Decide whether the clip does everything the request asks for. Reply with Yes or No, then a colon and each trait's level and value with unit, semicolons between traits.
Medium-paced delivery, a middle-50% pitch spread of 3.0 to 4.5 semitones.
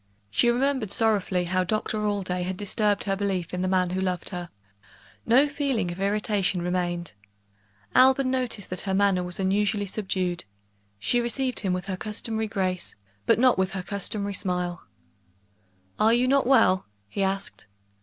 Yes: average, 160 wpm; average, 3.3 semitones